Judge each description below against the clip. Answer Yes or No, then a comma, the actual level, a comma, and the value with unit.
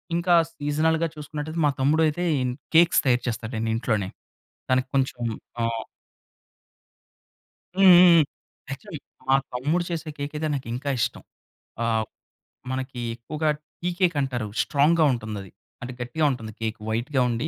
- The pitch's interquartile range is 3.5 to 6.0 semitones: Yes, average, 4.8 semitones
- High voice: No, medium, 140 Hz